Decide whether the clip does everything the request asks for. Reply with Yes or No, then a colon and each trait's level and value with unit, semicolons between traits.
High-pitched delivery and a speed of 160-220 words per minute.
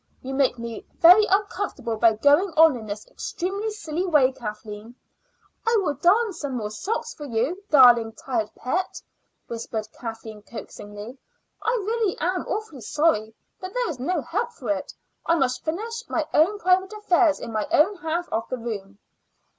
Yes: very high, 295 Hz; average, 165 wpm